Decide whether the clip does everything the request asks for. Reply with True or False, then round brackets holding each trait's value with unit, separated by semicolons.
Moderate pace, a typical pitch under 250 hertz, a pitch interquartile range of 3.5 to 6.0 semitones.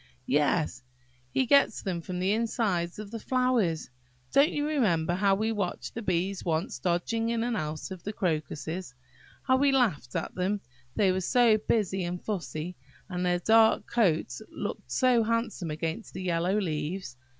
True (165 wpm; 190 Hz; 4.9 semitones)